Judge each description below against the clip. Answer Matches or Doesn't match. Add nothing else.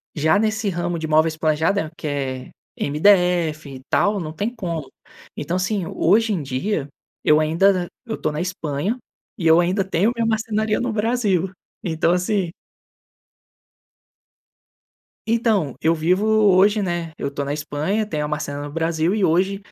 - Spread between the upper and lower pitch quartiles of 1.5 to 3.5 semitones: Doesn't match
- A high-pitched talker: Doesn't match